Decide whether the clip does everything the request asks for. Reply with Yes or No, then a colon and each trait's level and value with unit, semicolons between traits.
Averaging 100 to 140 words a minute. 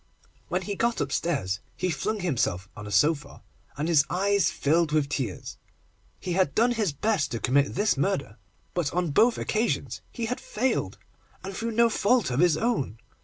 No: average, 175 wpm